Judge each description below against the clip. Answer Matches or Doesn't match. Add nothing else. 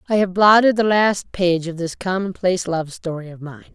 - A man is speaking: Doesn't match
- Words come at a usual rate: Doesn't match